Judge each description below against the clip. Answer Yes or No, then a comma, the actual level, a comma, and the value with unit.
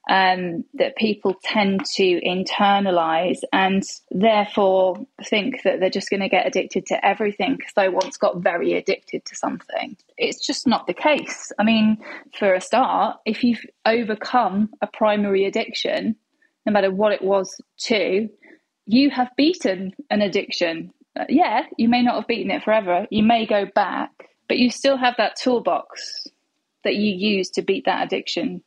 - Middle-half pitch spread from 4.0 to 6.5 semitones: Yes, average, 5.1 semitones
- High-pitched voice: Yes, high, 215 Hz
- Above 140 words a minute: Yes, average, 165 wpm